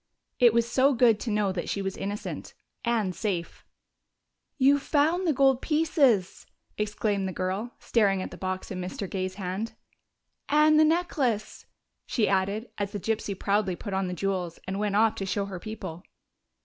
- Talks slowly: No, average, 175 wpm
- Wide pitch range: No, average, 4.3 semitones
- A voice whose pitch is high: Yes, high, 210 Hz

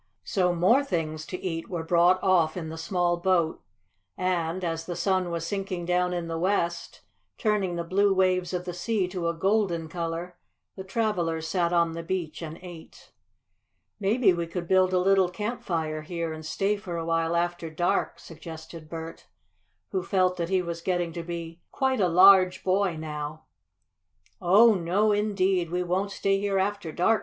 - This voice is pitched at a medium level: Yes, medium, 175 Hz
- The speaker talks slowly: No, average, 175 wpm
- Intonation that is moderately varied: No, narrow, 2.3 semitones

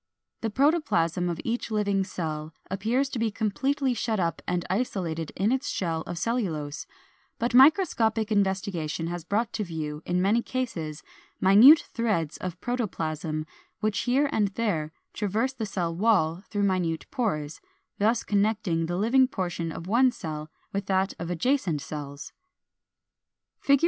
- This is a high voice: Yes, high, 195 Hz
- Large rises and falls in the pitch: Yes, wide, 5.8 semitones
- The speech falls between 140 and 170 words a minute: Yes, average, 150 wpm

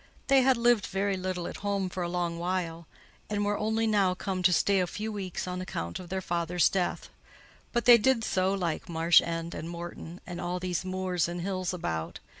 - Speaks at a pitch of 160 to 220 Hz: Yes, medium, 185 Hz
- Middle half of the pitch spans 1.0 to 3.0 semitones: Yes, narrow, 2.4 semitones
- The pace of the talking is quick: Yes, fast, 210 wpm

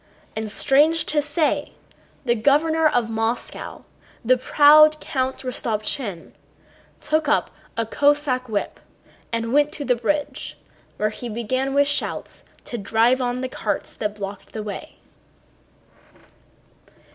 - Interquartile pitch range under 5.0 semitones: Yes, average, 4.6 semitones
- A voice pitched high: Yes, very high, 255 Hz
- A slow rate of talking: Yes, slow, 125 wpm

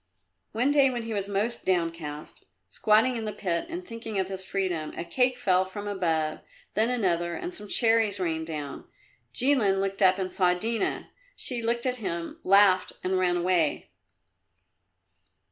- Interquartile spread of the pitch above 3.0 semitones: Yes, average, 4.4 semitones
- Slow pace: No, average, 160 wpm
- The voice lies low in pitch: No, high, 195 Hz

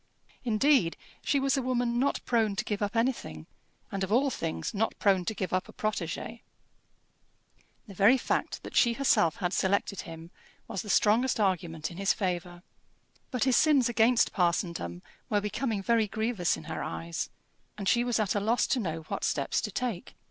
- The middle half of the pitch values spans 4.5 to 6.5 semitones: Yes, average, 5.1 semitones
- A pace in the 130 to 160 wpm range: No, average, 185 wpm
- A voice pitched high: Yes, high, 210 Hz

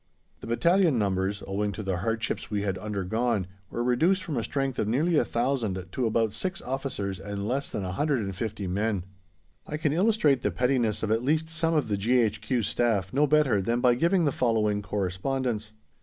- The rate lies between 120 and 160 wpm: No, average, 180 wpm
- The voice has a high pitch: No, low, 115 Hz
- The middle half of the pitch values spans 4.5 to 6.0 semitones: Yes, average, 5.2 semitones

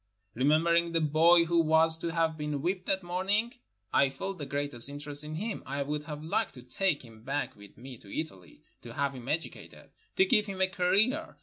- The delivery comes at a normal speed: No, fast, 215 wpm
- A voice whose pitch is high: No, medium, 160 Hz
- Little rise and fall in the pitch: No, average, 4.3 semitones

